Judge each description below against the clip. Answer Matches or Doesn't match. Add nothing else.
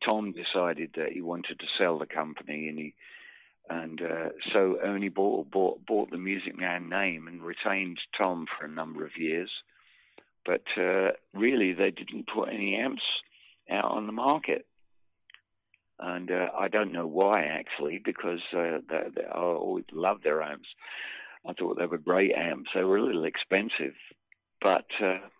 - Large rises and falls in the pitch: Doesn't match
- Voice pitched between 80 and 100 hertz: Matches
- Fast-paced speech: Doesn't match